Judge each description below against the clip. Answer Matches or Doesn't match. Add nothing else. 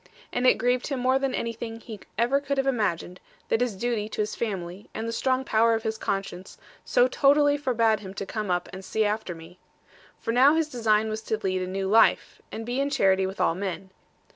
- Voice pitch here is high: Matches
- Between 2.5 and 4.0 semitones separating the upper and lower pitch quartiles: Doesn't match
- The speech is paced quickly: Matches